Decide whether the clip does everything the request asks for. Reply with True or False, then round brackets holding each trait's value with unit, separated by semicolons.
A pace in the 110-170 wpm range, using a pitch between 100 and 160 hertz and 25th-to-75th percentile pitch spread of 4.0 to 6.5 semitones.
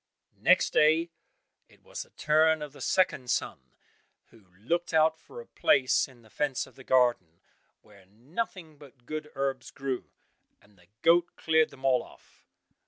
True (165 wpm; 140 Hz; 4.7 semitones)